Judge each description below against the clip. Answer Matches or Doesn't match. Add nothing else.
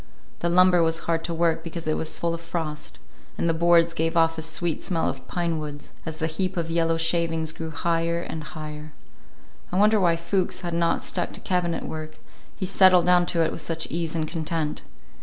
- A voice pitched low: Doesn't match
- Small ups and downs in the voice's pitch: Matches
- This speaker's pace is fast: Matches